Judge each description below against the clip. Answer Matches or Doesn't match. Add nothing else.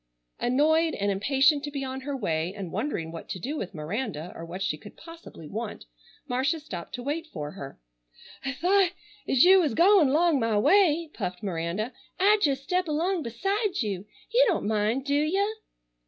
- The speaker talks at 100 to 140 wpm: Doesn't match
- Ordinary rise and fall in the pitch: Doesn't match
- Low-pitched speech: Doesn't match